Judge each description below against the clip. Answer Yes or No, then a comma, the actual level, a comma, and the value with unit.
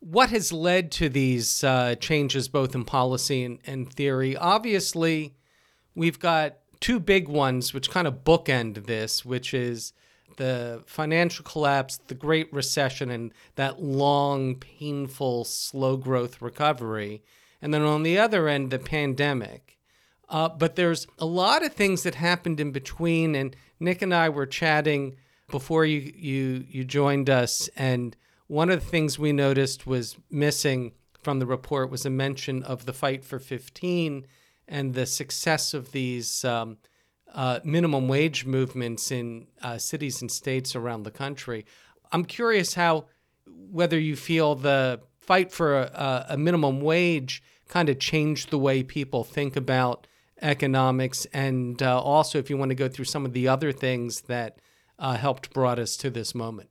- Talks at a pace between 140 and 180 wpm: Yes, average, 160 wpm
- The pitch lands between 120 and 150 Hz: Yes, medium, 140 Hz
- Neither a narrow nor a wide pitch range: Yes, average, 3.3 semitones